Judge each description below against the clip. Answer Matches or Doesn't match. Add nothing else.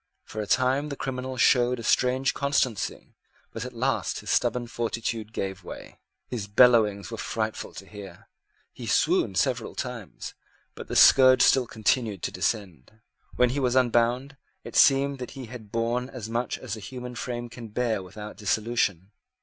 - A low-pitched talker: Matches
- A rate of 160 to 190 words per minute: Matches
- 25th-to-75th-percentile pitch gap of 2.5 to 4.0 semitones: Matches